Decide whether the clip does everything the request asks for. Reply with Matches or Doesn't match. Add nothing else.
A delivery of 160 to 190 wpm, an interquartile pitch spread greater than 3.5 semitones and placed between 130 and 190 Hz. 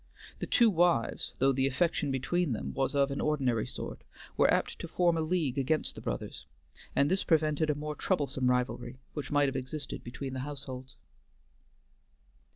Doesn't match